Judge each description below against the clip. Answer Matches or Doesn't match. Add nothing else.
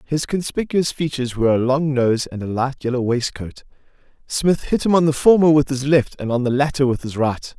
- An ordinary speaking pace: Doesn't match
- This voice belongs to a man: Matches